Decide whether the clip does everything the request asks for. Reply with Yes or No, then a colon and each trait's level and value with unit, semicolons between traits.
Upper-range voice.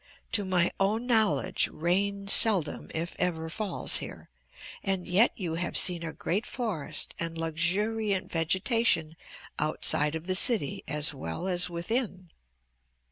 No: medium, 180 Hz